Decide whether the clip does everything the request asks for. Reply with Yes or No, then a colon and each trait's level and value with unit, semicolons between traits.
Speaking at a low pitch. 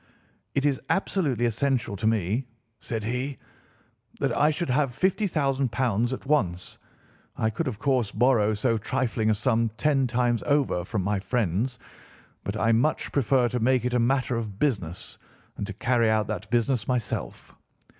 Yes: low, 120 Hz